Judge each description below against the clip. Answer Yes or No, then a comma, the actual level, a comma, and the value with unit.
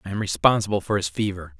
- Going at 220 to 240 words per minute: Yes, fast, 225 wpm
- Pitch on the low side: Yes, very low, 95 Hz